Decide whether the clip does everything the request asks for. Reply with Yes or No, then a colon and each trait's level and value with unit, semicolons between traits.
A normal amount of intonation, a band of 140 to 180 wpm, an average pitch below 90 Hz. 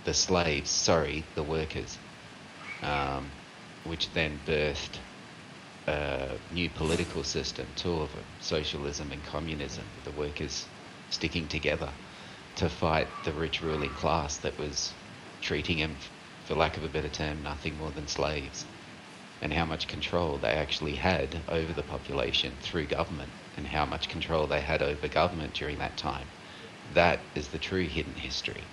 No: narrow, 2.2 semitones; average, 150 wpm; very low, 80 Hz